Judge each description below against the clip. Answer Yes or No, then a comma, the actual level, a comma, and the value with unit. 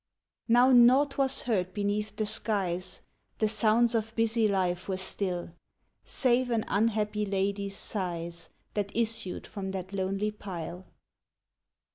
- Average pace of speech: No, slow, 125 wpm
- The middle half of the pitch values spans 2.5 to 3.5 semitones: Yes, average, 3.1 semitones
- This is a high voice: Yes, high, 205 Hz